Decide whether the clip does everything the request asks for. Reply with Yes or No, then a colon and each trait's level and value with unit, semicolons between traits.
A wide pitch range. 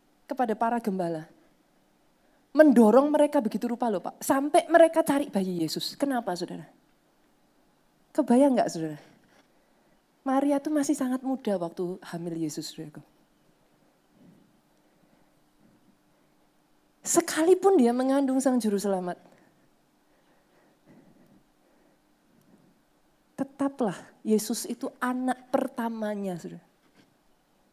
Yes: wide, 6.7 semitones